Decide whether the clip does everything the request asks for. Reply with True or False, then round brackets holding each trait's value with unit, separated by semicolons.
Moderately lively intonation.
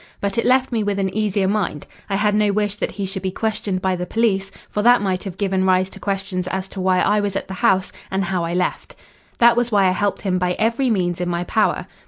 False (2.3 semitones)